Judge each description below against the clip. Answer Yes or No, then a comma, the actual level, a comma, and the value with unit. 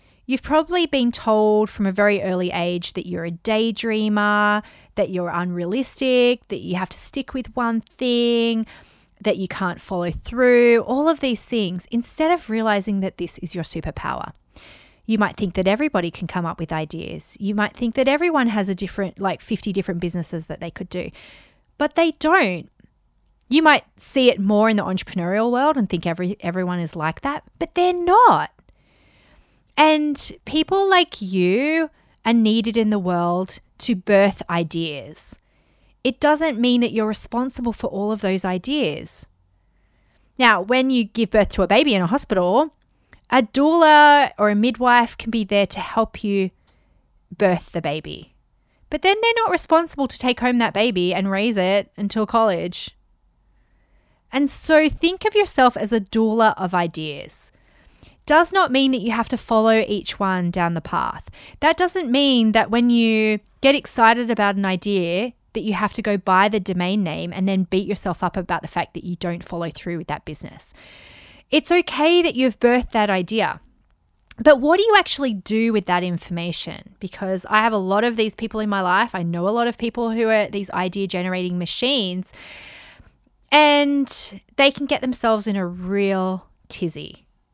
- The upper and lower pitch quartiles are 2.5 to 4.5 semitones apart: No, wide, 5.6 semitones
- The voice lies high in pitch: Yes, high, 215 Hz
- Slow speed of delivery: No, average, 180 wpm